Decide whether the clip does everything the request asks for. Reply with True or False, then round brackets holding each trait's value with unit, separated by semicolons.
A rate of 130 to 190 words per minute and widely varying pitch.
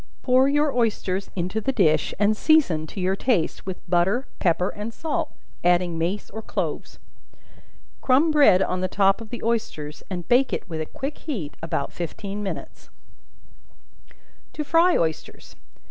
True (155 wpm; 6.4 semitones)